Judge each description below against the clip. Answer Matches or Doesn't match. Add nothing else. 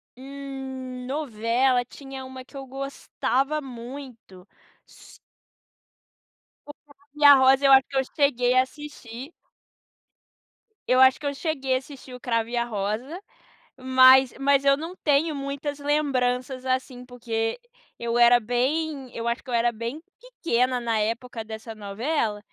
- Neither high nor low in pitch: Doesn't match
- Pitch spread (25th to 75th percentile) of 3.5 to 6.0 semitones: Doesn't match